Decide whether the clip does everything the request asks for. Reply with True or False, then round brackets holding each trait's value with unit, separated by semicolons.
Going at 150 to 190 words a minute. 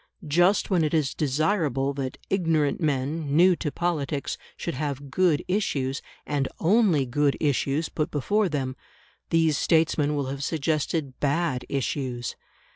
False (135 wpm)